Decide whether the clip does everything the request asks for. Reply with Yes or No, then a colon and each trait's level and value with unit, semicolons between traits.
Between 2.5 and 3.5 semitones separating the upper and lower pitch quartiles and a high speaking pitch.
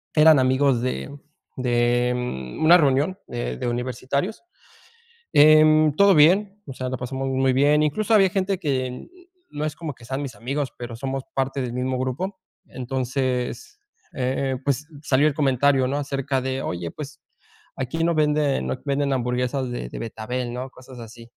No: average, 2.9 semitones; low, 135 Hz